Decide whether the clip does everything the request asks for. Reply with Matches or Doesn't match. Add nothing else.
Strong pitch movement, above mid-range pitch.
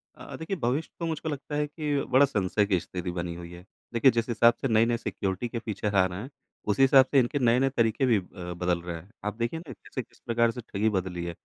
Doesn't match